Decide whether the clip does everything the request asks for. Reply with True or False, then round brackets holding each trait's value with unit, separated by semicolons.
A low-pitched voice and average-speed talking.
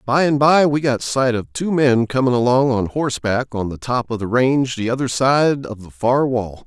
False (125 Hz; 235 wpm)